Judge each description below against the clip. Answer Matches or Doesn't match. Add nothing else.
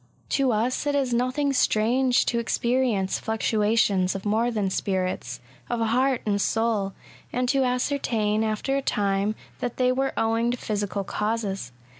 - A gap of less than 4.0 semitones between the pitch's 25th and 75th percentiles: Matches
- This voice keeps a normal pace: Matches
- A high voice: Matches